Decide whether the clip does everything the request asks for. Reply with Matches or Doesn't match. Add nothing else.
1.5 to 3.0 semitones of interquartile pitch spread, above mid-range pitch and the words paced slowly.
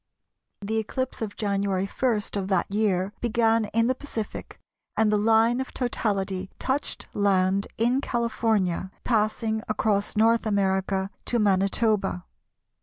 Matches